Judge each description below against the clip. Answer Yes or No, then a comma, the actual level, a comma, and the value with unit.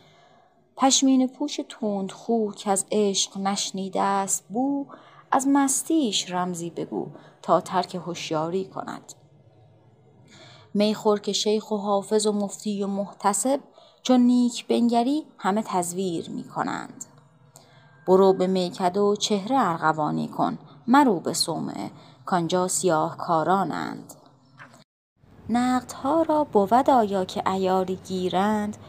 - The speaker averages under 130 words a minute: Yes, average, 110 wpm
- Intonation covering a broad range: No, average, 4.7 semitones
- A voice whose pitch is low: No, high, 195 Hz